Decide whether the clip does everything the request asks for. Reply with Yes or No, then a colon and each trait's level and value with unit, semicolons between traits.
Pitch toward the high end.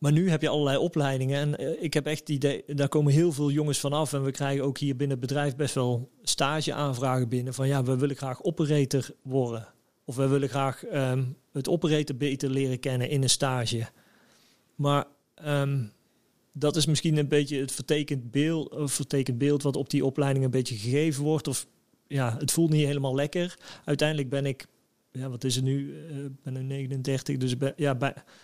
No: medium, 140 Hz